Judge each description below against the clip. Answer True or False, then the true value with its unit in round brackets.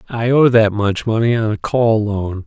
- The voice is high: False (110 Hz)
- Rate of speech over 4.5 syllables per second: False (4.4 syllables/s)